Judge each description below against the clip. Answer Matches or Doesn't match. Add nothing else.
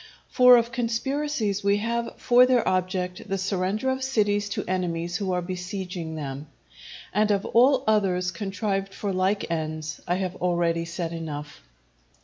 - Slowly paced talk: Doesn't match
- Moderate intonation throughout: Matches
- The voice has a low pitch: Doesn't match